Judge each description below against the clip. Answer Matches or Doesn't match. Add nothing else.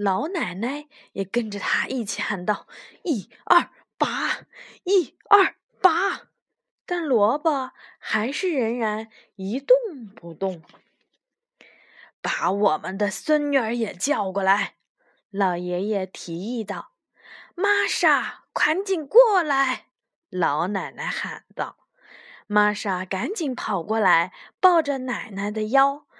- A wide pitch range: Matches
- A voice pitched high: Matches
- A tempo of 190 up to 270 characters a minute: Doesn't match